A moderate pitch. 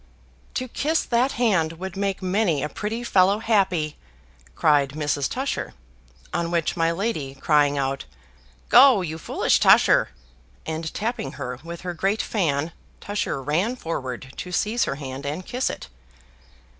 Yes: medium, 170 Hz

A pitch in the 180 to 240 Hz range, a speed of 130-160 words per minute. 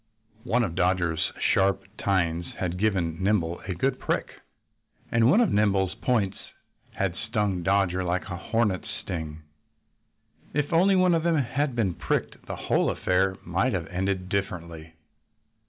No: very low, 95 Hz; average, 145 wpm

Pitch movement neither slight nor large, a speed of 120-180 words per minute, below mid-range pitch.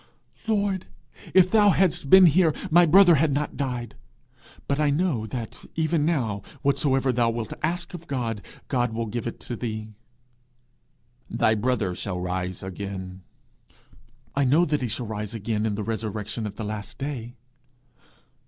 No: wide, 6.2 semitones; average, 155 wpm; low, 120 Hz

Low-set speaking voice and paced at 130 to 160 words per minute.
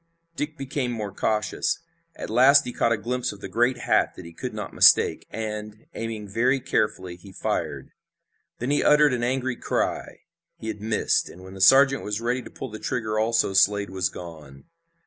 No: low, 110 Hz; average, 190 wpm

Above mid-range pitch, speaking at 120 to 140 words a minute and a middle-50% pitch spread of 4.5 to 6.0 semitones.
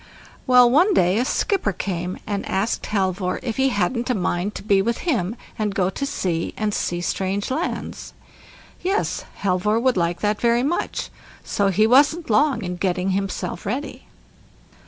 No: high, 210 Hz; average, 165 wpm; average, 5.2 semitones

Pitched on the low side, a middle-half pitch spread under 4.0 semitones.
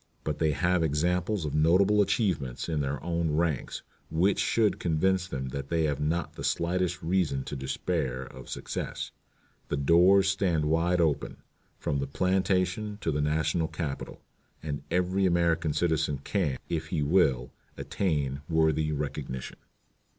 Yes: very low, 80 Hz; average, 3.6 semitones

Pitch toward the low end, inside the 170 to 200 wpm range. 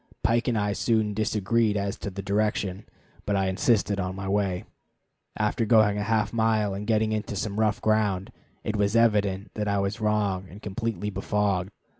Yes: low, 105 Hz; average, 180 wpm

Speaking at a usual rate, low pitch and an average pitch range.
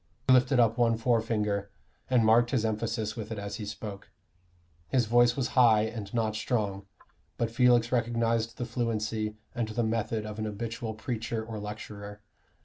No: average, 165 wpm; low, 115 Hz; narrow, 1.8 semitones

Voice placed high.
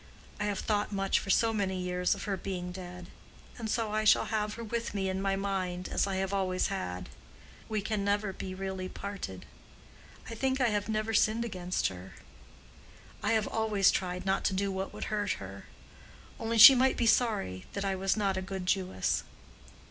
Yes: high, 195 Hz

